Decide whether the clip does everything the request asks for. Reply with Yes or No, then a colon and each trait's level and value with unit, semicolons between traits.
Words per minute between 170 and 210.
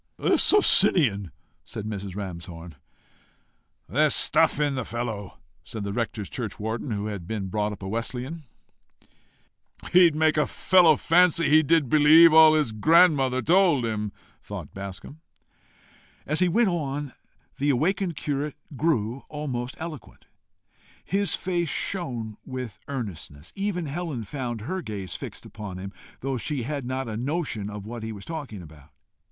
No: average, 145 wpm